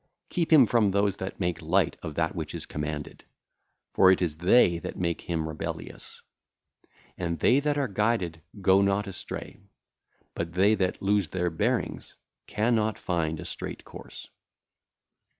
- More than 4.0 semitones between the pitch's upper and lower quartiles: No, average, 3.7 semitones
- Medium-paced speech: Yes, average, 150 wpm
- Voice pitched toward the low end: Yes, very low, 95 Hz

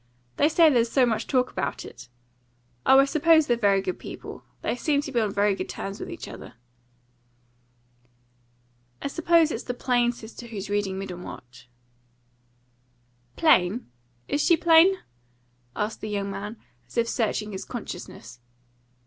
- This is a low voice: No, high, 235 Hz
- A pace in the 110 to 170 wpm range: Yes, average, 150 wpm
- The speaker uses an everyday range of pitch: No, wide, 6.1 semitones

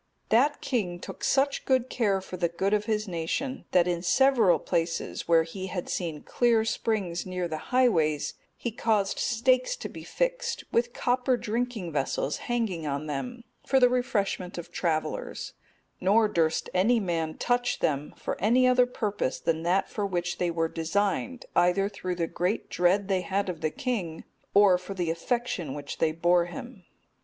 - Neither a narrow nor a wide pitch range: No, wide, 5.8 semitones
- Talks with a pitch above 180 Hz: Yes, high, 190 Hz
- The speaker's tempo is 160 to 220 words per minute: Yes, average, 170 wpm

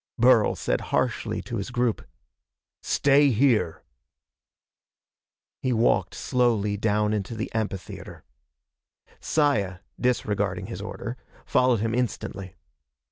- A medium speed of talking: No, slow, 100 wpm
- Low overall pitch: Yes, low, 115 Hz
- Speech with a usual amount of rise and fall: Yes, average, 3.4 semitones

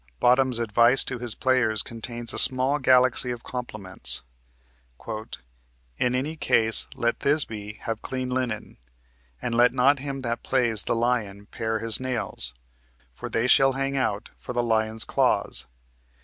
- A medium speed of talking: Yes, average, 145 wpm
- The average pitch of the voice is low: Yes, low, 120 Hz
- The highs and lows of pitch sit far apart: No, average, 2.7 semitones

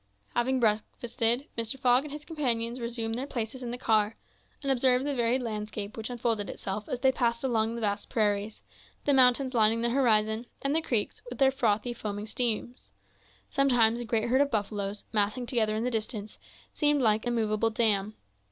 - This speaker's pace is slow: No, average, 185 wpm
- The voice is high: Yes, high, 235 Hz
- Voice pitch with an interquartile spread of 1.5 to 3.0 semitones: Yes, average, 2.7 semitones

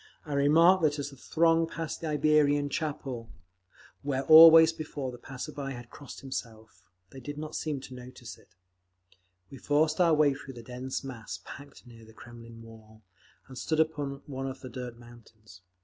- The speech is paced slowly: No, average, 175 wpm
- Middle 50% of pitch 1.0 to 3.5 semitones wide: No, average, 4.0 semitones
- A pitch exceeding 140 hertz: No, low, 135 Hz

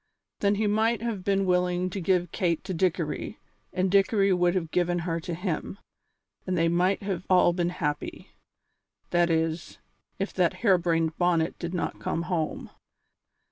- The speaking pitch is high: No, medium, 180 Hz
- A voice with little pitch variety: Yes, narrow, 2.2 semitones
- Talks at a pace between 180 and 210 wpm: No, average, 165 wpm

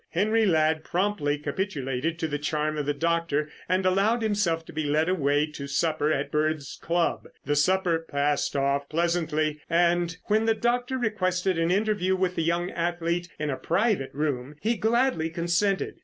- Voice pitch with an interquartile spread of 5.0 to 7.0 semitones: No, average, 4.0 semitones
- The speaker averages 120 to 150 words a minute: No, average, 170 wpm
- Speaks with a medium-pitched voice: Yes, medium, 165 Hz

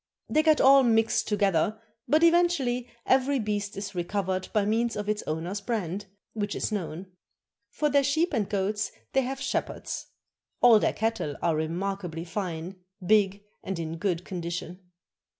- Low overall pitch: No, high, 205 Hz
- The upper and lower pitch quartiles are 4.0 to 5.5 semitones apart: Yes, average, 5.2 semitones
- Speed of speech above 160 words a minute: No, average, 150 wpm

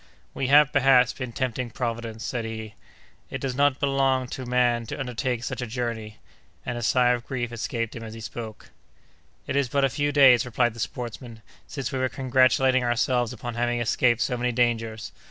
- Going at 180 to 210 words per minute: Yes, average, 190 wpm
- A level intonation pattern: Yes, narrow, 1.9 semitones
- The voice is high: No, low, 125 Hz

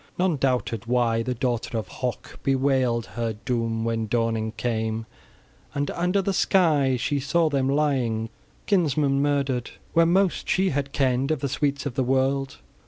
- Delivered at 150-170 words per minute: Yes, average, 160 wpm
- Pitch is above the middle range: No, low, 135 Hz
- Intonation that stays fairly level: No, average, 3.6 semitones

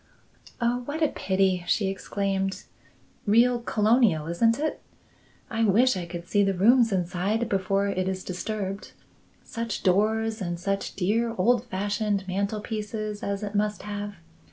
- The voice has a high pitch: Yes, high, 205 Hz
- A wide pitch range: No, average, 2.8 semitones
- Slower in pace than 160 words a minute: Yes, average, 140 wpm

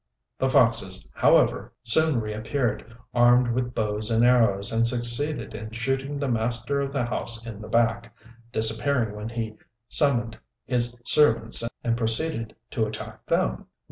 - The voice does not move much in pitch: Yes, narrow, 2.0 semitones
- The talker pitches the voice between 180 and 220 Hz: No, low, 115 Hz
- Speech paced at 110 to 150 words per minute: Yes, average, 140 wpm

